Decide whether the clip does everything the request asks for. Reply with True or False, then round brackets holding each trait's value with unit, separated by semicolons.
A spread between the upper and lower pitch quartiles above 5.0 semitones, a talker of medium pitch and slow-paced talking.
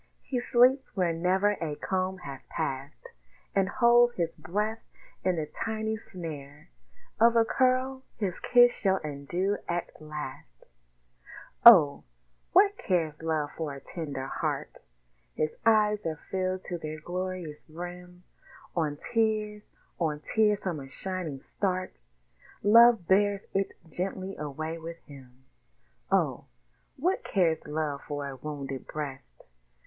True (5.6 semitones; 180 Hz; 130 wpm)